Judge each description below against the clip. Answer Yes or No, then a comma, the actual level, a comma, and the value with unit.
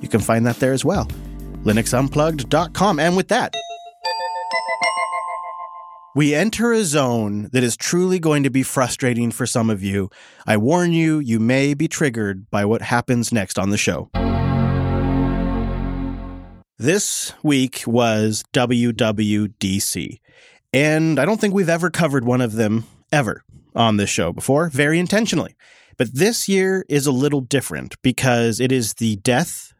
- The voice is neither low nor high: No, low, 130 Hz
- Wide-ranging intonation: Yes, wide, 6.6 semitones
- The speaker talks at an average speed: Yes, average, 145 wpm